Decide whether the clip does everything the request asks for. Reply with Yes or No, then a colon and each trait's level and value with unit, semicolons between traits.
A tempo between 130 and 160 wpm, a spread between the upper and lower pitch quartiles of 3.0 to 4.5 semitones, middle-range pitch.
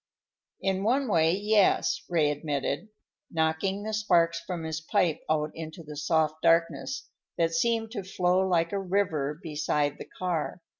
Yes: average, 150 wpm; average, 3.5 semitones; medium, 170 Hz